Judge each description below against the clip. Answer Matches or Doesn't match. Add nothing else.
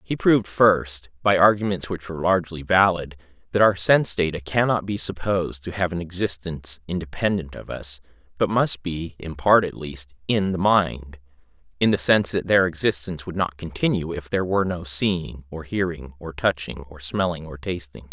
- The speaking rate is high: Doesn't match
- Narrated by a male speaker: Matches